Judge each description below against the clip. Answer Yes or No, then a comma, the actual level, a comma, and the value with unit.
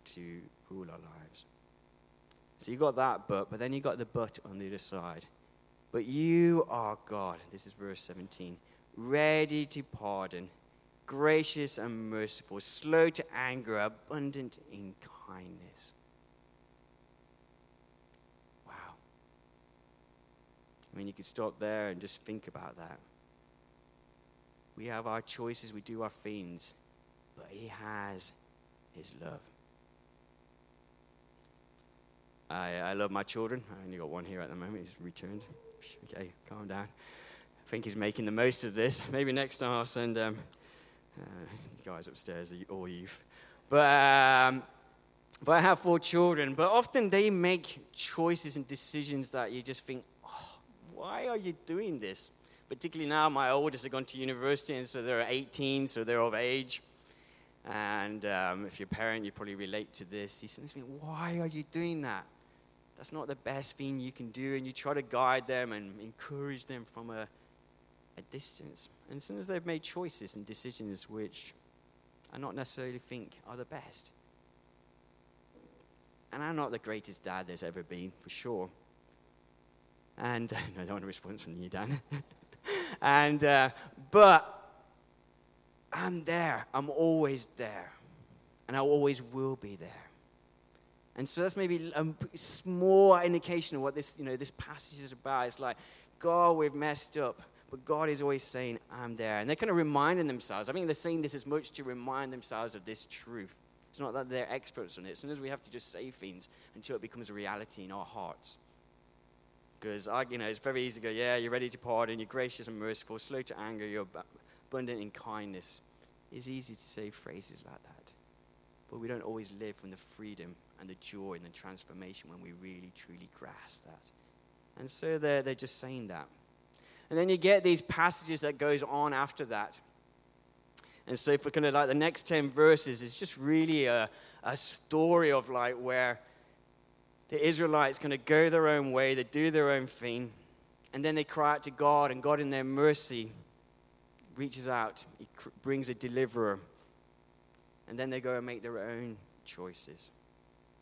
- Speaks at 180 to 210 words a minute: No, average, 170 wpm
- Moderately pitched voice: No, low, 110 Hz